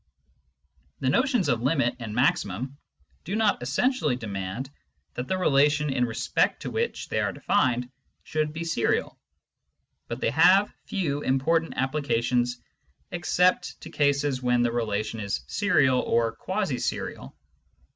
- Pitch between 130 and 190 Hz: Yes, low, 135 Hz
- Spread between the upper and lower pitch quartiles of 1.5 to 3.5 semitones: No, average, 5.1 semitones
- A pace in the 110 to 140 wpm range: Yes, slow, 135 wpm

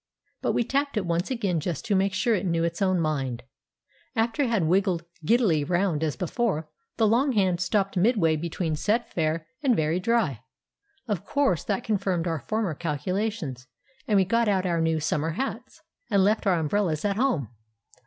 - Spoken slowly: No, average, 185 wpm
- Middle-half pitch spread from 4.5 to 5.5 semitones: Yes, average, 5.2 semitones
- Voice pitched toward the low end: No, medium, 185 Hz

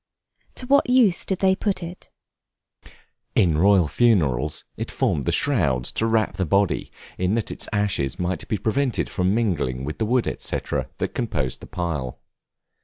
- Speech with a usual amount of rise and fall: No, wide, 7.9 semitones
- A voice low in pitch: Yes, low, 100 Hz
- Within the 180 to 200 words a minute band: No, average, 165 wpm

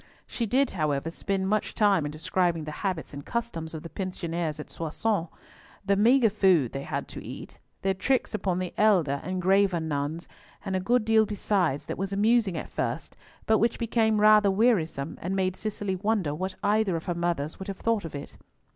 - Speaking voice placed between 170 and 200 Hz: Yes, high, 190 Hz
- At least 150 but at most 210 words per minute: Yes, average, 195 wpm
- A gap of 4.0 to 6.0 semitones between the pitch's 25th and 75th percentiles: Yes, average, 4.5 semitones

